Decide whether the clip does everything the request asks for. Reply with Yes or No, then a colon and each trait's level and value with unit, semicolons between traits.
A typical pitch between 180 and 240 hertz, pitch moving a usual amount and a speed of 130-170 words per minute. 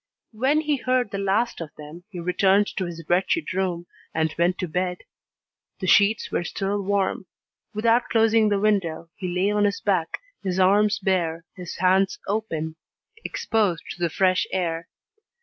Yes: high, 190 Hz; average, 3.1 semitones; average, 165 wpm